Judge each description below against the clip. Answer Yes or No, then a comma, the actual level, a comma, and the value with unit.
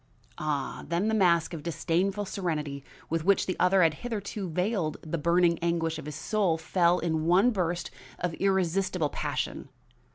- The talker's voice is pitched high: No, medium, 170 Hz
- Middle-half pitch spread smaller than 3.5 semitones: Yes, average, 2.9 semitones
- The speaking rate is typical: Yes, average, 160 wpm